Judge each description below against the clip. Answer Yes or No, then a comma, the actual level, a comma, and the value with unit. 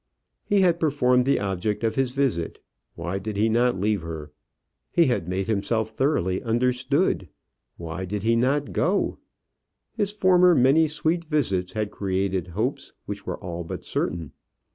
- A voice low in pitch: Yes, low, 115 Hz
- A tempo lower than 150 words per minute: No, average, 155 wpm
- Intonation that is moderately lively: No, wide, 7.3 semitones